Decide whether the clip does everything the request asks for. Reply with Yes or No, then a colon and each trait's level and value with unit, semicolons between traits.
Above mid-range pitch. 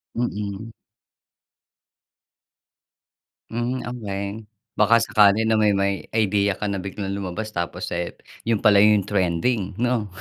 No: low, 105 Hz